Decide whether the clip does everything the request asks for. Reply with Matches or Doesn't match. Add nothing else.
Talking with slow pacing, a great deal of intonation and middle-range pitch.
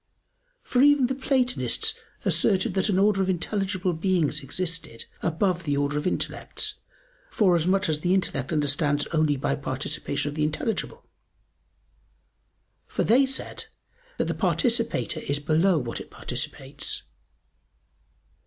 Matches